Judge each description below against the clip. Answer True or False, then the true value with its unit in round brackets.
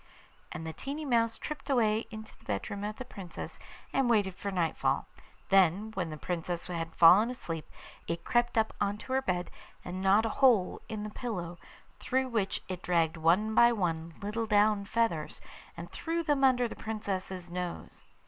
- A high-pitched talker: True (205 Hz)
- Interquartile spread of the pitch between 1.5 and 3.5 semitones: False (4.7 semitones)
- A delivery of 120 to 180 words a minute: True (175 wpm)